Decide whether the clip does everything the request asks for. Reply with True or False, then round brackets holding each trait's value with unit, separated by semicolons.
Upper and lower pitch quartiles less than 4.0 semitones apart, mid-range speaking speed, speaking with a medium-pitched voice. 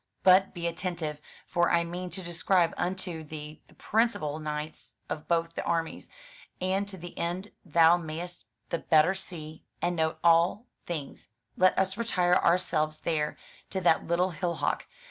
True (2.4 semitones; 155 wpm; 170 Hz)